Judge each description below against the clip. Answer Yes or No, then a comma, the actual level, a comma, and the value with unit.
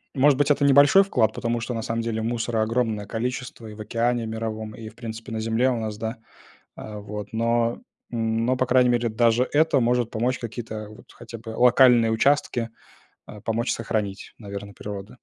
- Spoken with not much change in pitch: Yes, narrow, 1.9 semitones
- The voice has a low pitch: Yes, low, 115 Hz